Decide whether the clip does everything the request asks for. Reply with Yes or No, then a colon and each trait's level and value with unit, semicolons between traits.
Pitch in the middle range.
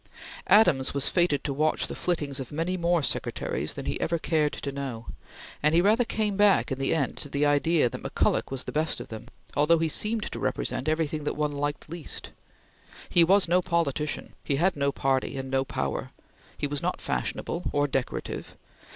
Yes: medium, 150 Hz